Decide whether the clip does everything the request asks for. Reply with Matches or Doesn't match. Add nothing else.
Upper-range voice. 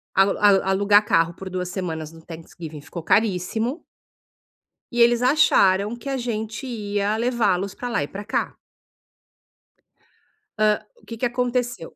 Matches